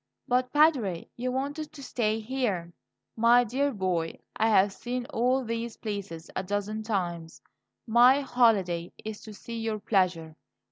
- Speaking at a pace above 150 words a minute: No, average, 145 wpm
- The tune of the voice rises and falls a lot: No, average, 4.8 semitones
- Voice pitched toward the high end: Yes, high, 220 Hz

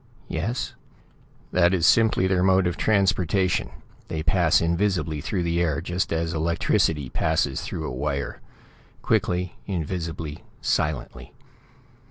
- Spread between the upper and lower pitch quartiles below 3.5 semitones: Yes, average, 2.9 semitones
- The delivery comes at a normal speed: No, slow, 120 wpm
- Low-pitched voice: Yes, very low, 85 Hz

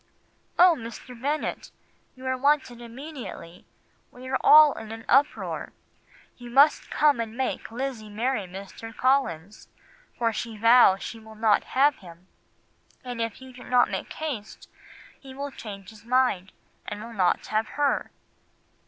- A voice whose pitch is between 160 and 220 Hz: No, high, 240 Hz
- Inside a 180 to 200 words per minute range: No, average, 145 wpm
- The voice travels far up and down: No, average, 3.7 semitones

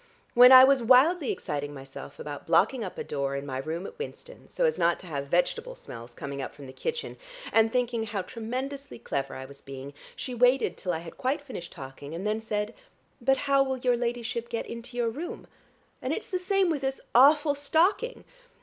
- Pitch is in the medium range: No, high, 235 Hz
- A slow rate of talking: No, fast, 205 wpm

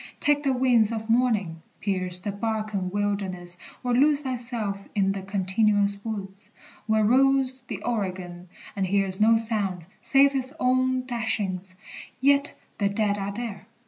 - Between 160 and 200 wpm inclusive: No, average, 145 wpm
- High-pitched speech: Yes, high, 215 Hz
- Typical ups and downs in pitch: Yes, average, 4.3 semitones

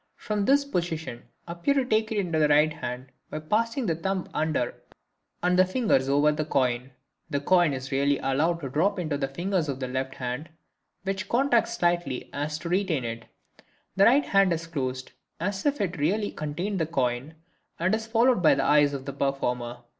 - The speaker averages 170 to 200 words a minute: Yes, average, 195 wpm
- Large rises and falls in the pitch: Yes, wide, 6.1 semitones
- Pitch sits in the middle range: Yes, medium, 160 Hz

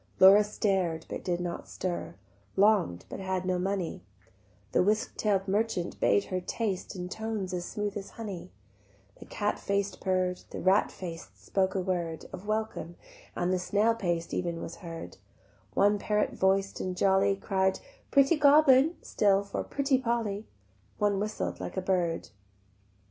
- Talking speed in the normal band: Yes, average, 155 wpm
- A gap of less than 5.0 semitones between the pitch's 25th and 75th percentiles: Yes, narrow, 2.6 semitones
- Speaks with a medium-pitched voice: No, high, 195 Hz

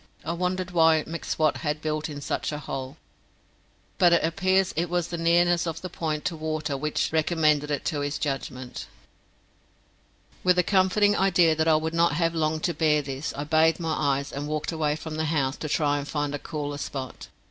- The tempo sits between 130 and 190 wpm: No, average, 200 wpm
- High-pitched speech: No, medium, 155 Hz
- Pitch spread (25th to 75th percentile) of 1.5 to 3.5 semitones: Yes, narrow, 2.4 semitones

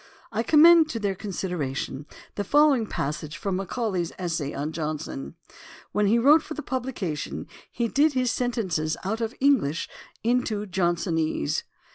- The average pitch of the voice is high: Yes, high, 200 Hz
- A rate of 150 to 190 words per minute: No, slow, 135 wpm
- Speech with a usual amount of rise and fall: No, wide, 7.6 semitones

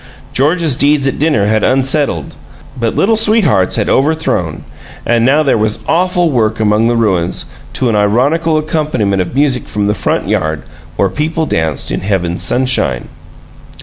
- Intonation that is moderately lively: No, wide, 6.7 semitones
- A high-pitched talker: No, low, 120 Hz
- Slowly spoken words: No, average, 155 wpm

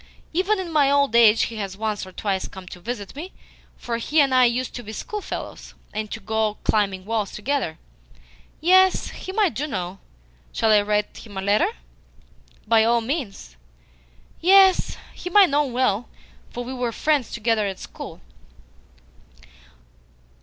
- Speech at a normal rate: Yes, average, 160 wpm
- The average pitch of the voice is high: Yes, high, 235 Hz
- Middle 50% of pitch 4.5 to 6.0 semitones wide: Yes, wide, 5.6 semitones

